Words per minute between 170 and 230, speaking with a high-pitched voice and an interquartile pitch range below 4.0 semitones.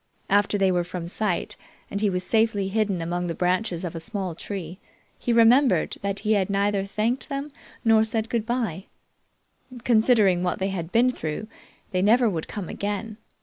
Yes: average, 180 wpm; high, 200 Hz; average, 3.5 semitones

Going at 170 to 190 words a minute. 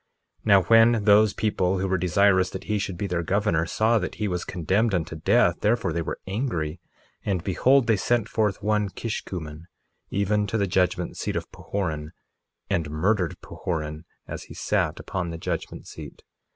Yes: average, 180 wpm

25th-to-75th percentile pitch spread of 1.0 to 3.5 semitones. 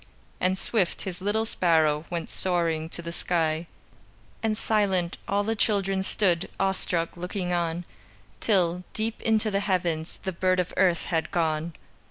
Yes: average, 2.8 semitones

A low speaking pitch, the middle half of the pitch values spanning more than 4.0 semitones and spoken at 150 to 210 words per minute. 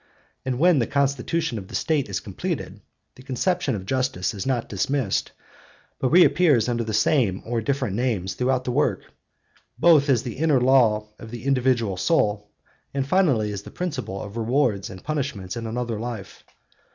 Yes: low, 125 Hz; average, 4.5 semitones; average, 170 wpm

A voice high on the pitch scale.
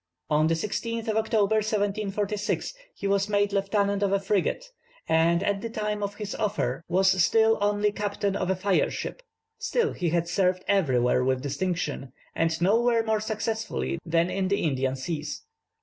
Yes: high, 200 Hz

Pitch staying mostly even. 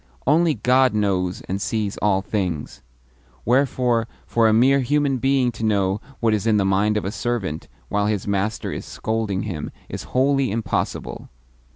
No: average, 4.2 semitones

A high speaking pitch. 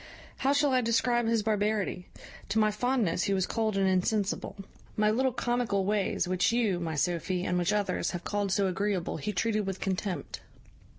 Yes: high, 205 Hz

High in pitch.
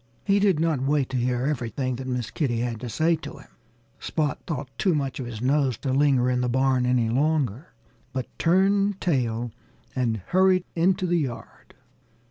No: low, 135 Hz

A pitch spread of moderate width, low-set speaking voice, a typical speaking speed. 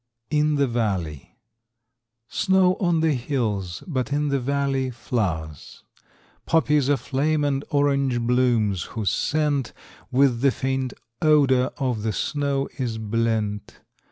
No: average, 4.1 semitones; low, 130 Hz; slow, 120 wpm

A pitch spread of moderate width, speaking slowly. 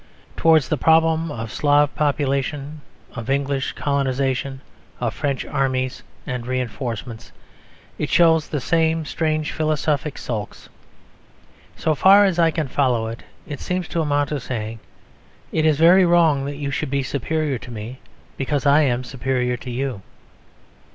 No: average, 3.4 semitones; average, 145 wpm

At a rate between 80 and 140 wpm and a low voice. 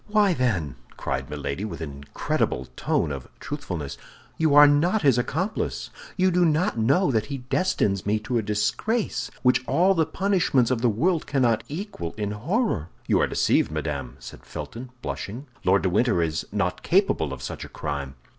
No: average, 175 wpm; low, 120 Hz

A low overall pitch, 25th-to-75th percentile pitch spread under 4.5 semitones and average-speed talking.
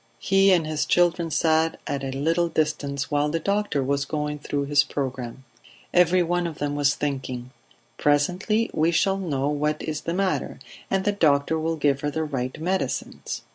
No: medium, 150 Hz; average, 3.4 semitones; average, 175 wpm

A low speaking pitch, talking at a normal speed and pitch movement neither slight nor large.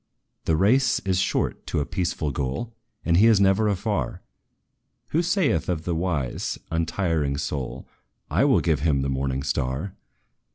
No: very low, 85 Hz; average, 155 wpm; wide, 5.9 semitones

